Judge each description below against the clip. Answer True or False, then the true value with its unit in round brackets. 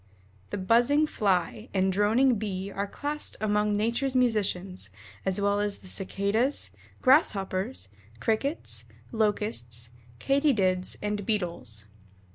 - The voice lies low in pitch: False (205 Hz)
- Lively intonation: False (3.7 semitones)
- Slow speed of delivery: True (105 wpm)